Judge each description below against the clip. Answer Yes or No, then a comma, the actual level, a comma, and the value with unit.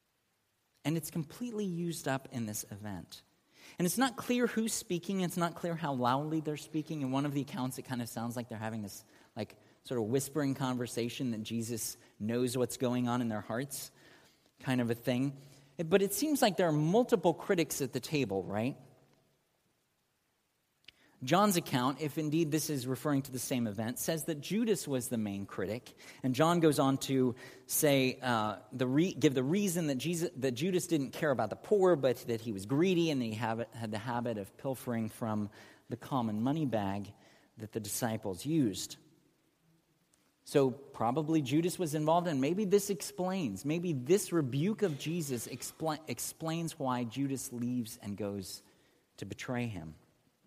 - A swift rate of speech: Yes, fast, 175 wpm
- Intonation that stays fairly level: No, average, 5.3 semitones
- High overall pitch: No, low, 135 Hz